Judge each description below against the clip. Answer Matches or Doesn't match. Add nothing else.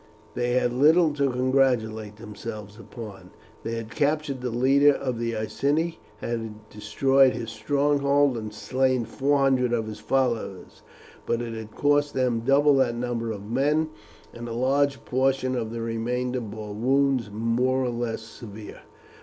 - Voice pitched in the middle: Doesn't match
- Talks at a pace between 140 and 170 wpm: Matches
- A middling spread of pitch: Matches